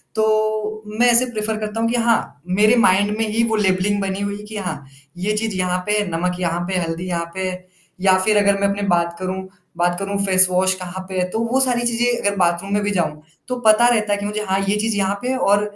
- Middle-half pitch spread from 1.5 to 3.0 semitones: Yes, average, 2.7 semitones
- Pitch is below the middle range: No, high, 200 Hz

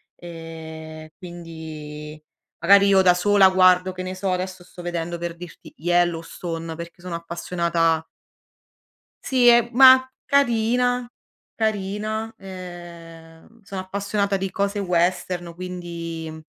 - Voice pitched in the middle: Yes, medium, 180 Hz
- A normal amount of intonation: Yes, average, 3.0 semitones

